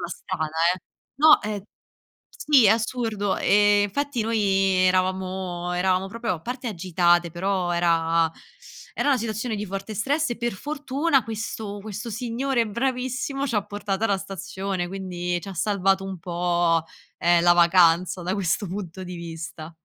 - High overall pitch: Yes, high, 195 Hz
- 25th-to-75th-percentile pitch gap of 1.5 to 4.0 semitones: No, average, 4.4 semitones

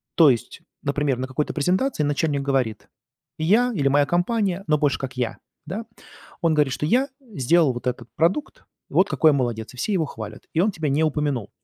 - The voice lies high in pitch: No, medium, 150 Hz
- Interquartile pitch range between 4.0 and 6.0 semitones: Yes, average, 4.6 semitones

